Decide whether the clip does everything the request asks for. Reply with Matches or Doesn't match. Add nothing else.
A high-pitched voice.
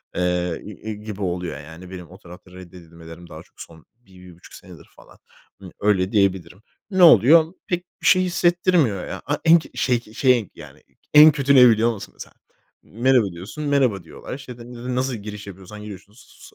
Doesn't match